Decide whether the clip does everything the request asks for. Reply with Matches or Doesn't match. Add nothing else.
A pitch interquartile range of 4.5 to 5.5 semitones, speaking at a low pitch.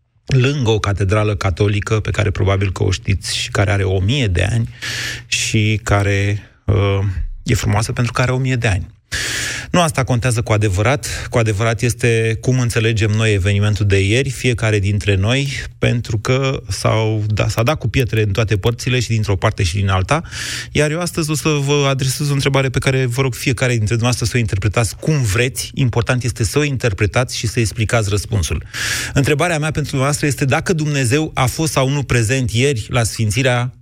Doesn't match